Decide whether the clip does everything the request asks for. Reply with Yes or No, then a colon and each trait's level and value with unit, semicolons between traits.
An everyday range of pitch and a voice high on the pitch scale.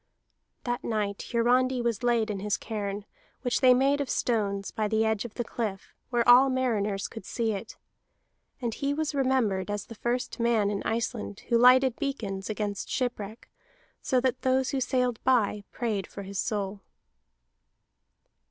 Yes: average, 3.5 semitones; high, 230 Hz